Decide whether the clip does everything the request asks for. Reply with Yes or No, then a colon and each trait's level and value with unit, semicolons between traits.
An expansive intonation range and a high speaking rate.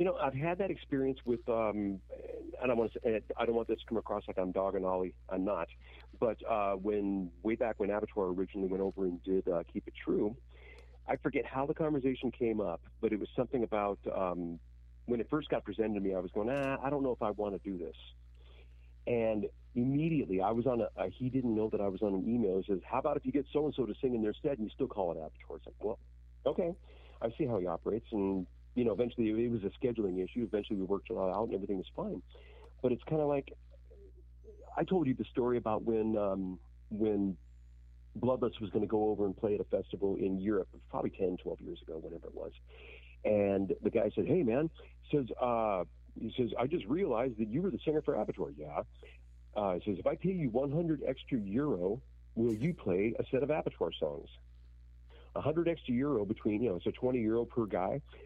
Yes: wide, 7.8 semitones; fast, 235 wpm